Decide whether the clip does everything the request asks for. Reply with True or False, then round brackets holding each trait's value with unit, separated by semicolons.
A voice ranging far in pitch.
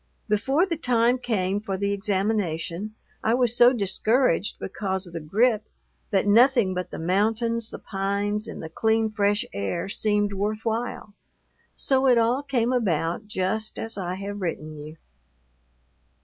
False (3.3 semitones)